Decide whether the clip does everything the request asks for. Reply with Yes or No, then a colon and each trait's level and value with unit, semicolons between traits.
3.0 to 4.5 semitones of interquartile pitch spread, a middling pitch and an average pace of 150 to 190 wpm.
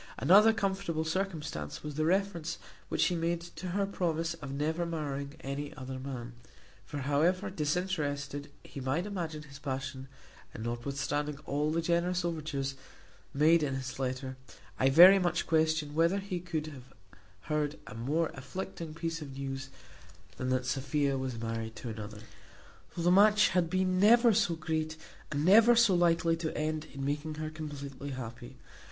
Yes: average, 3.9 semitones; medium, 155 Hz; average, 160 wpm